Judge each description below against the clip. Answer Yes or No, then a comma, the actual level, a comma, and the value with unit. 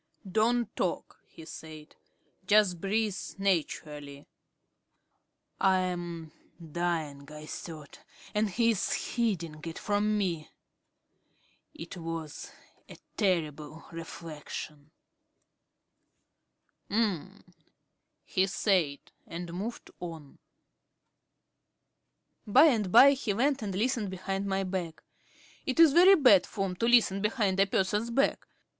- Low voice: No, high, 190 Hz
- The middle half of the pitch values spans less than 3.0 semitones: No, average, 4.5 semitones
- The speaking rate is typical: No, slow, 105 wpm